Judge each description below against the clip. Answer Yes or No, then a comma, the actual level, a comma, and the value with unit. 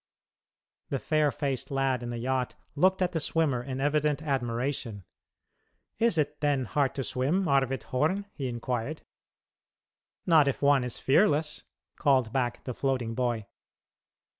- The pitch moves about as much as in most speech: Yes, average, 3.1 semitones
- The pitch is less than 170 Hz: Yes, low, 135 Hz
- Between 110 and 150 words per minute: Yes, average, 140 wpm